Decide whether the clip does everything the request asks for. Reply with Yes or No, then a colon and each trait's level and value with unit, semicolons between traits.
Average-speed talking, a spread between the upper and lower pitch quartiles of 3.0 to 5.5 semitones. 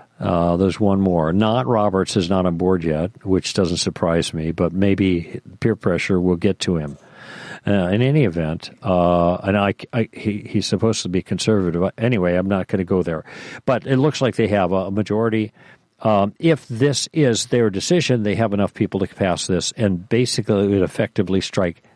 Yes: average, 195 wpm; average, 3.8 semitones